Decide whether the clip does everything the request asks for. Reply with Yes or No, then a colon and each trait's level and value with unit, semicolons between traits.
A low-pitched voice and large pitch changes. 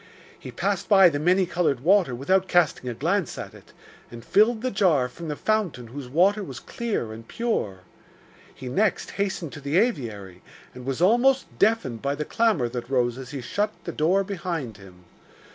No: medium, 155 Hz; wide, 8.0 semitones